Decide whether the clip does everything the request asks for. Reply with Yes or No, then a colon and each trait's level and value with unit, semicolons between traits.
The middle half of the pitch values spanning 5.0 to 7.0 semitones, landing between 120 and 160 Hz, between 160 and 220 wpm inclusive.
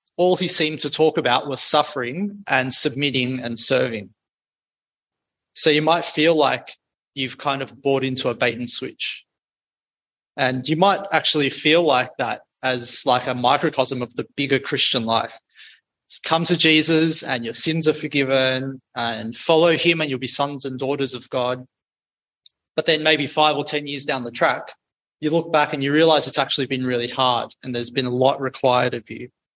No: average, 3.5 semitones; medium, 140 Hz; average, 185 wpm